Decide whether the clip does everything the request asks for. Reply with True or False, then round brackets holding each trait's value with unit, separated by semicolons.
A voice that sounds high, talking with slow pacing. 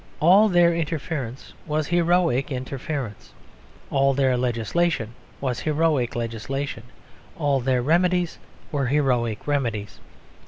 False (140 Hz; 105 wpm)